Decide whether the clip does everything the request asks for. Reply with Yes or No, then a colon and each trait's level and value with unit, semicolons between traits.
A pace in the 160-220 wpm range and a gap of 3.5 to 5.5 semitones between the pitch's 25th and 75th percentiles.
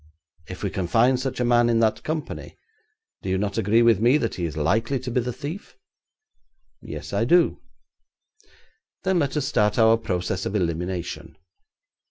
Yes: average, 175 wpm; average, 4.9 semitones